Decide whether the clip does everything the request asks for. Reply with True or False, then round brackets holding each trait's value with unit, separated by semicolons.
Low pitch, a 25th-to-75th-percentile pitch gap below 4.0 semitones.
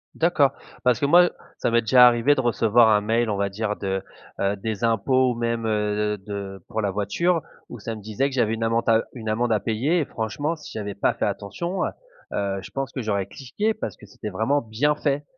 False (115 Hz; 4.3 semitones)